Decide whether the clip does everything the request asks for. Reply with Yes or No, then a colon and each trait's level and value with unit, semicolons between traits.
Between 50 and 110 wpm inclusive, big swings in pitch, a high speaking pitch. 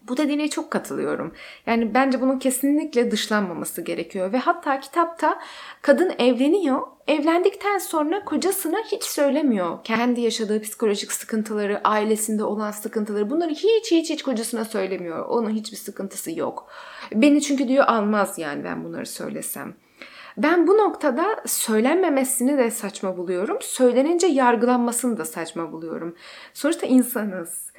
No: average, 125 wpm; wide, 6.1 semitones; very high, 255 Hz